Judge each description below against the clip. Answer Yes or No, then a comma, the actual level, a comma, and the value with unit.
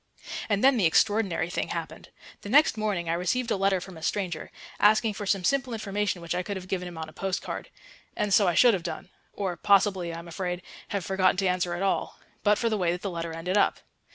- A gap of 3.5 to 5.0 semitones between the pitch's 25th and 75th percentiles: No, average, 2.9 semitones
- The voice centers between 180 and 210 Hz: Yes, high, 190 Hz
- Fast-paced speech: Yes, fast, 240 wpm